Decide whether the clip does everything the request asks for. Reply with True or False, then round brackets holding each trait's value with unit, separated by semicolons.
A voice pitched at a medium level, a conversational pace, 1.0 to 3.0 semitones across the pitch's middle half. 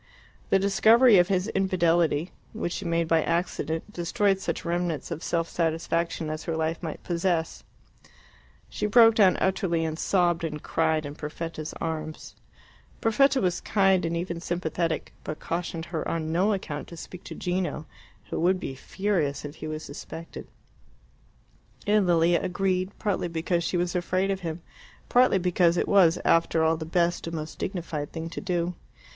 True (170 Hz; 165 wpm; 2.5 semitones)